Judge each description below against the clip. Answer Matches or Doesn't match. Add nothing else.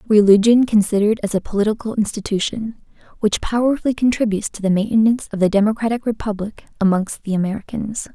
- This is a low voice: Doesn't match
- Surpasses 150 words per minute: Doesn't match